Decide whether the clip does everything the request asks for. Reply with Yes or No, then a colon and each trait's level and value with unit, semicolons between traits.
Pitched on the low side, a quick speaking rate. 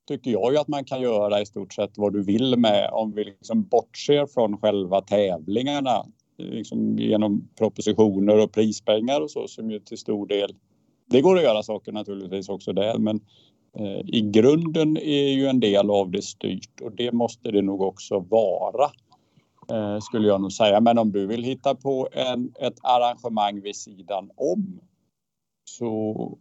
No: low, 110 Hz; average, 175 wpm